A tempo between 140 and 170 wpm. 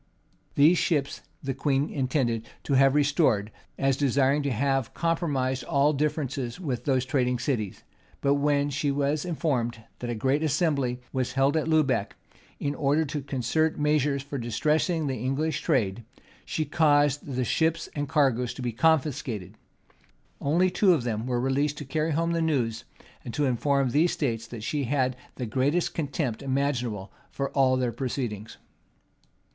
Yes: average, 160 wpm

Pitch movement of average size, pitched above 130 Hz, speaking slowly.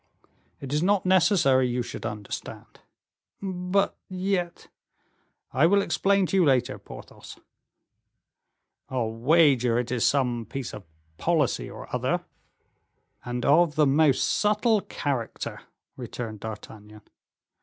No: wide, 7.0 semitones; medium, 140 Hz; slow, 120 wpm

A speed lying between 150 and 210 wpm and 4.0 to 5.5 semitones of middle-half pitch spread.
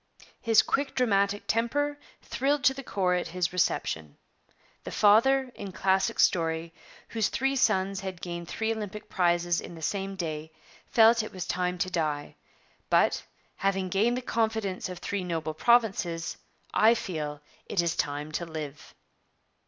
Yes: average, 155 wpm; average, 4.6 semitones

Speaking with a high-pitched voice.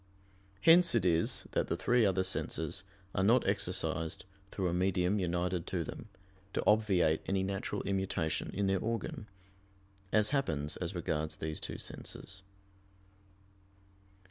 No: very low, 95 Hz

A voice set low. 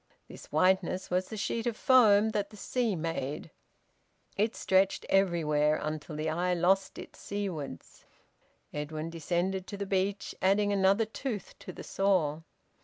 No: high, 190 Hz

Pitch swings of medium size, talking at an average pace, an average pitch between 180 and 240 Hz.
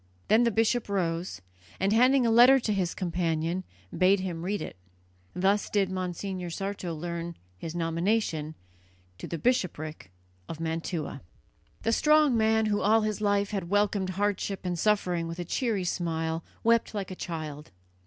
Yes: average, 4.1 semitones; average, 160 wpm; high, 190 Hz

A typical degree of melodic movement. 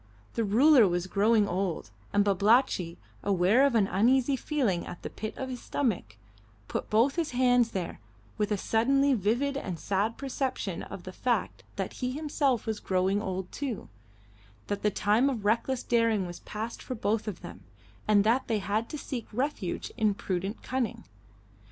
Yes: average, 4.4 semitones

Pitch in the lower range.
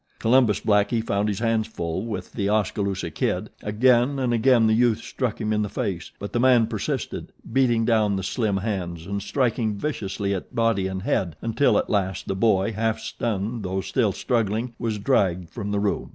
Yes: low, 105 Hz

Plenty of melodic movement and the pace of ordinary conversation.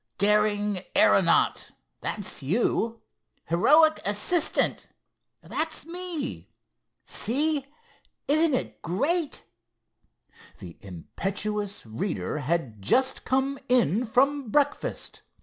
No: wide, 6.8 semitones; slow, 75 wpm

